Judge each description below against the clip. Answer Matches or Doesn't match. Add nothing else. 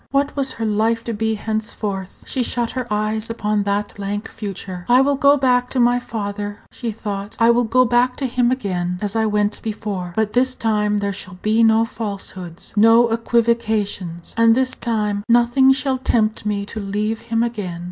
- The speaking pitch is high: Matches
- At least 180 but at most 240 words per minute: Matches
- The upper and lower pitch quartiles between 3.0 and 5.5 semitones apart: Doesn't match